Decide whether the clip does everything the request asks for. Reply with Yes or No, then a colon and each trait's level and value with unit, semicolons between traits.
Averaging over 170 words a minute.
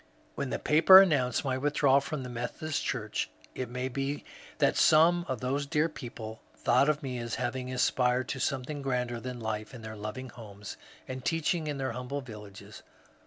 Yes: average, 185 wpm